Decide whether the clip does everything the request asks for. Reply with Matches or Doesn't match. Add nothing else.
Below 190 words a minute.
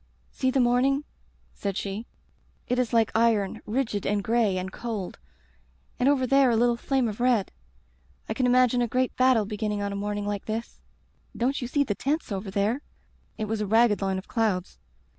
Doesn't match